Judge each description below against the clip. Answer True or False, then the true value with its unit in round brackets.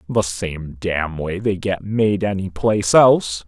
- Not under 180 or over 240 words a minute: False (170 wpm)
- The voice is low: True (95 Hz)